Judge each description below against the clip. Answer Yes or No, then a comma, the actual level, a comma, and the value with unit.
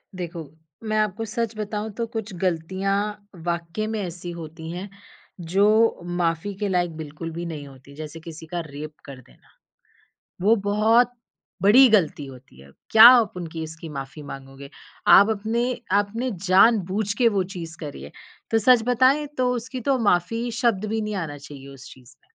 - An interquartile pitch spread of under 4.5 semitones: No, wide, 5.4 semitones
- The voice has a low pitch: No, high, 190 Hz